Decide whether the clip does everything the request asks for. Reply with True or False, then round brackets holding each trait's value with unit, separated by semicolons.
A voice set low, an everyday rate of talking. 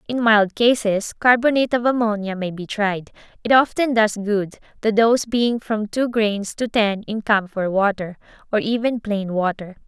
False (215 Hz; 170 wpm)